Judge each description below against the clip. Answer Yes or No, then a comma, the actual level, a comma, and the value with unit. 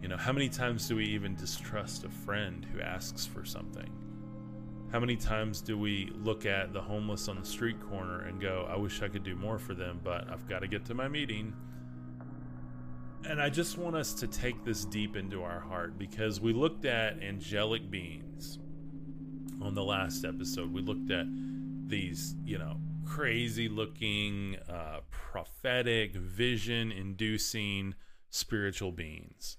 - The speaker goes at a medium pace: Yes, average, 165 wpm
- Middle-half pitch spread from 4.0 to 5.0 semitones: Yes, average, 4.4 semitones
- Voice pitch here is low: Yes, low, 105 Hz